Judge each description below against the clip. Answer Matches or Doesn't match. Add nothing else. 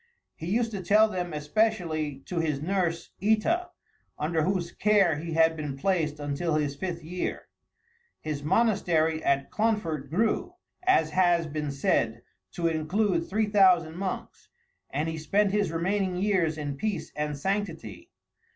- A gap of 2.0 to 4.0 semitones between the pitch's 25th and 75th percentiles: Doesn't match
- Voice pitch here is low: Doesn't match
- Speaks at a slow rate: Doesn't match